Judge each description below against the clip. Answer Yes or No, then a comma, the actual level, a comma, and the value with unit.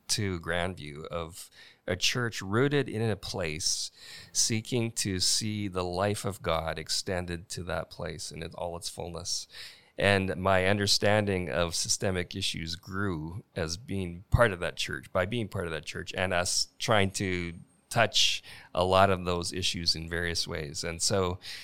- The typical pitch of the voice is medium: No, very low, 90 Hz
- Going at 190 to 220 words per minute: No, average, 165 wpm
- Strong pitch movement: No, average, 2.8 semitones